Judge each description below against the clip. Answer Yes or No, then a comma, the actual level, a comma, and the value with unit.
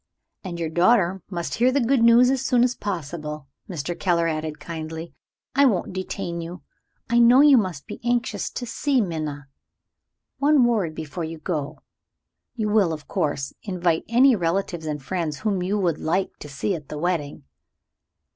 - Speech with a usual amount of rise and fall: No, wide, 6.5 semitones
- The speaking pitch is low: No, medium, 180 Hz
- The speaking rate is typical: Yes, average, 170 wpm